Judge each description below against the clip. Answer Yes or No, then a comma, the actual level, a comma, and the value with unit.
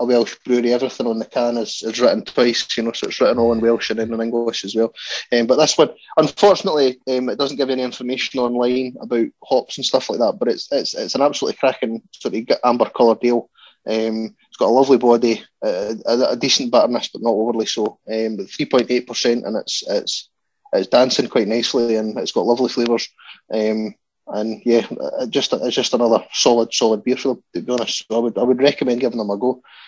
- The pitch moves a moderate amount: No, narrow, 1.8 semitones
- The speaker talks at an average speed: No, fast, 220 wpm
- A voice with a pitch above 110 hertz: Yes, low, 120 Hz